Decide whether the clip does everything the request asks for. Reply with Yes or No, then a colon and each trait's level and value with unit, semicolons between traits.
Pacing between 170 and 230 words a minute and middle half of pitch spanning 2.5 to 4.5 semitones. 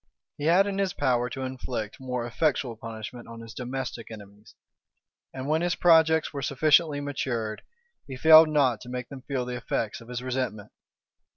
Yes: average, 180 wpm; average, 3.9 semitones